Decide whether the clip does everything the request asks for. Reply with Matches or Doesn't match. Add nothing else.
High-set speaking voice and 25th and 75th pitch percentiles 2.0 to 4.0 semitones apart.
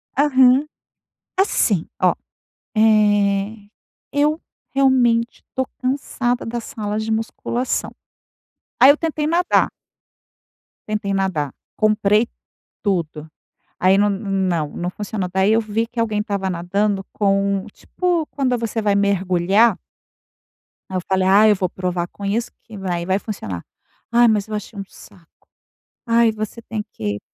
Matches